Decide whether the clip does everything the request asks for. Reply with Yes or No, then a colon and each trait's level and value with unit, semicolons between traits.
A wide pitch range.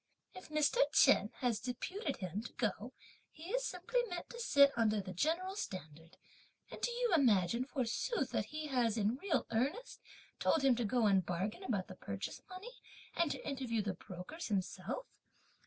Yes: wide, 8.8 semitones